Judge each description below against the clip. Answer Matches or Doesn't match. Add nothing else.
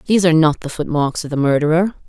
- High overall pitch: Doesn't match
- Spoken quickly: Matches